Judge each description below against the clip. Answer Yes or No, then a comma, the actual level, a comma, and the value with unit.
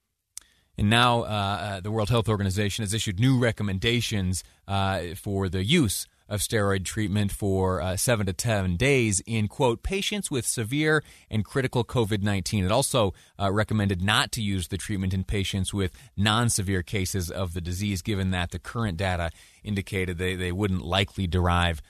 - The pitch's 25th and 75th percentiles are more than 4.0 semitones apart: No, average, 3.1 semitones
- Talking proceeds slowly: No, average, 170 wpm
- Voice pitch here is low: Yes, low, 100 Hz